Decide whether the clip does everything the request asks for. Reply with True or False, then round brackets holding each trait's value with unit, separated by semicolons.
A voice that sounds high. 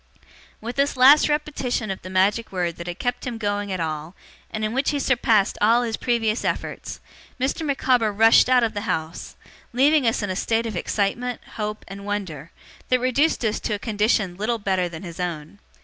True (215 Hz)